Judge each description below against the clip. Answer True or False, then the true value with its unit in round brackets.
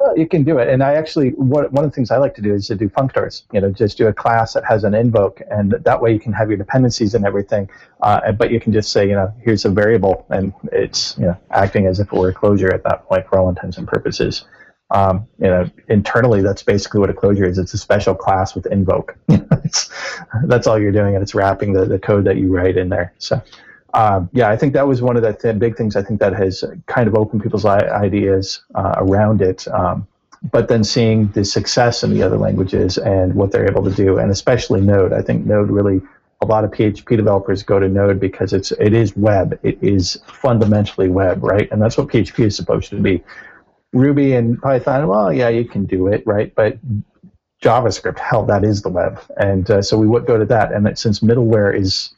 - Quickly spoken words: True (235 wpm)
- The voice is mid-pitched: False (105 Hz)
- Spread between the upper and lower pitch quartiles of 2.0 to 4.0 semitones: True (2.9 semitones)